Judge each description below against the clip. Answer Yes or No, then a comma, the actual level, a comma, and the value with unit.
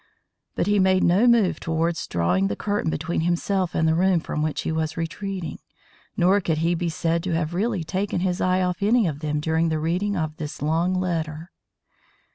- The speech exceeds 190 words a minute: Yes, average, 200 wpm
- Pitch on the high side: No, medium, 170 Hz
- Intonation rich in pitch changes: No, average, 2.8 semitones